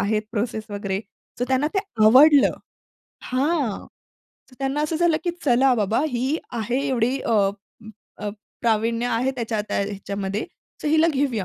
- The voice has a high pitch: Yes, high, 245 Hz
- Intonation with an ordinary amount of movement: Yes, average, 4.2 semitones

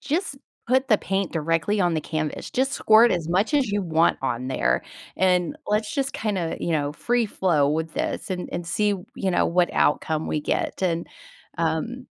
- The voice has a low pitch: No, medium, 180 Hz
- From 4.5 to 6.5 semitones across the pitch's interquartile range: Yes, average, 5.1 semitones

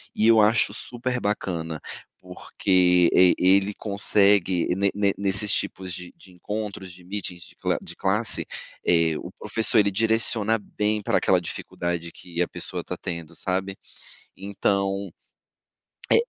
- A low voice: Yes, low, 100 Hz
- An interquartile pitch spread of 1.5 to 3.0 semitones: Yes, average, 2.7 semitones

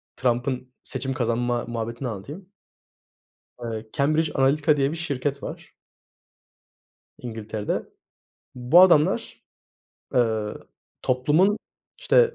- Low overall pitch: Yes, low, 130 Hz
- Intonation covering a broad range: No, average, 4.4 semitones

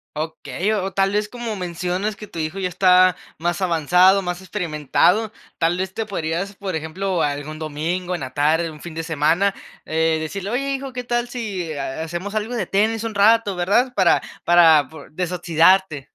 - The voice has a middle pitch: Yes, medium, 180 Hz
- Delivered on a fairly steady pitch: No, average, 3.9 semitones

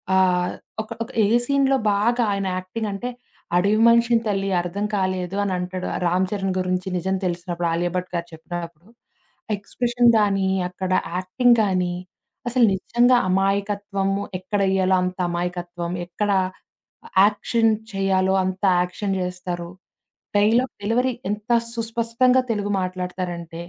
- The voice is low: No, high, 195 Hz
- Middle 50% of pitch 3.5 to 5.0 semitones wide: No, average, 2.9 semitones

